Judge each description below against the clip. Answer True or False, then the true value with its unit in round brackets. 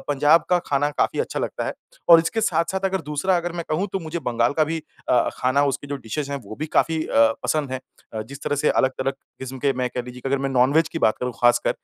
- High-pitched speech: False (145 Hz)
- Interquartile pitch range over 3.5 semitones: True (3.9 semitones)